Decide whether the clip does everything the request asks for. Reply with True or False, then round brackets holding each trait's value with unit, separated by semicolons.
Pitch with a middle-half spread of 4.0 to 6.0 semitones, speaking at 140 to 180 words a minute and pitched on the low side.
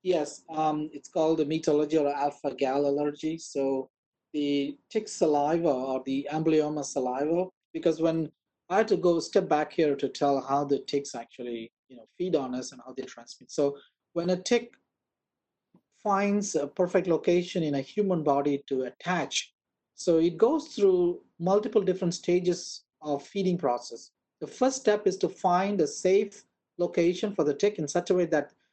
False (4.4 semitones; 175 wpm; 160 Hz)